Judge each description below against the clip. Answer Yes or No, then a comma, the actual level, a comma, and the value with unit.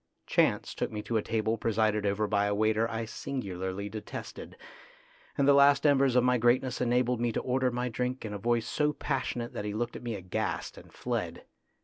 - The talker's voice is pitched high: No, low, 115 Hz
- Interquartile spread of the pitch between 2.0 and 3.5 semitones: Yes, average, 2.9 semitones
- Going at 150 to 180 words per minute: No, fast, 205 wpm